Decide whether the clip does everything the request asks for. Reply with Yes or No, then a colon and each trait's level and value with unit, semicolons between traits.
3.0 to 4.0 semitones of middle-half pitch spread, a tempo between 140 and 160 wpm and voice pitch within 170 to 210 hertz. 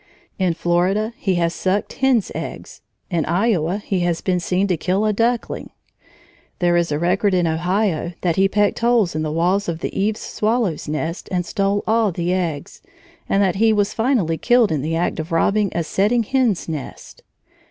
No: average, 3.7 semitones; average, 185 wpm; medium, 185 Hz